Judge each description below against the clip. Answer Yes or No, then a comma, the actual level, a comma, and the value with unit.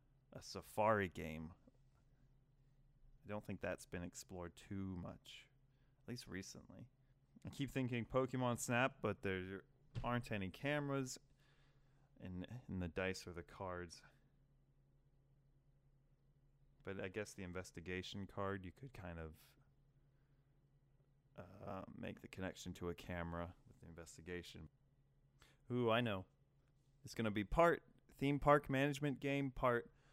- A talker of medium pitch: No, low, 130 Hz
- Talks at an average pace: No, slow, 125 wpm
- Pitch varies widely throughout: Yes, wide, 6.1 semitones